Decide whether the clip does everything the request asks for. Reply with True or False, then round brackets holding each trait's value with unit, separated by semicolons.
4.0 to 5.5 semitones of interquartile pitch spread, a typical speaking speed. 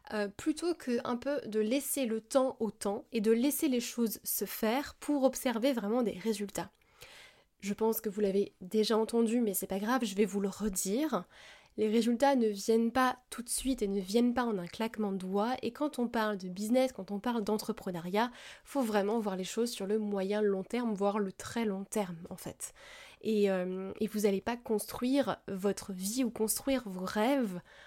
False (3.4 semitones; 210 wpm)